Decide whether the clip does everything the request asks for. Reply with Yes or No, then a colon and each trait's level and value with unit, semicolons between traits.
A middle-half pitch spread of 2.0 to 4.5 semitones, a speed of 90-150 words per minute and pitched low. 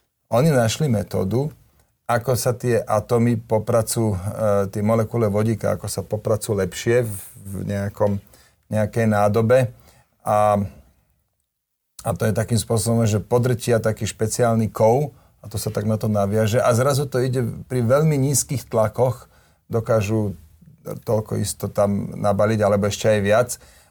Yes: narrow, 2.5 semitones; average, 135 wpm; low, 110 Hz